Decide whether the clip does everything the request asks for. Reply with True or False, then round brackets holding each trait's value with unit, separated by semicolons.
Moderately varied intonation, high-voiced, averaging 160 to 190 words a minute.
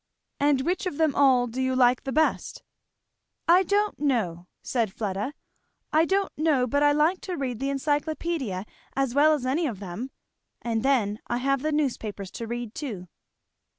True (4.6 semitones; 270 Hz; 175 wpm)